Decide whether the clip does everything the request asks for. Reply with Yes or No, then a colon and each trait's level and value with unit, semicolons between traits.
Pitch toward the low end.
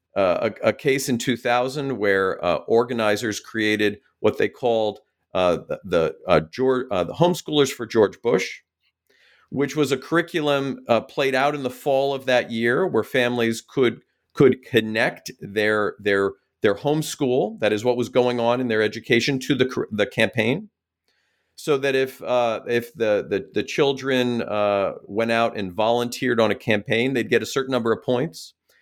Yes: low, 120 Hz